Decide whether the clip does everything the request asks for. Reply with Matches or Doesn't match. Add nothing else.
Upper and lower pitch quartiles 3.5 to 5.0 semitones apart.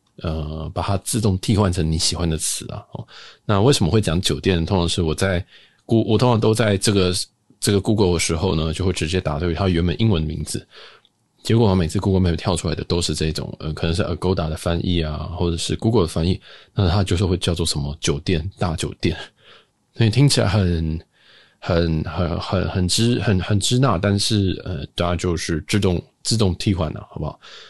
Matches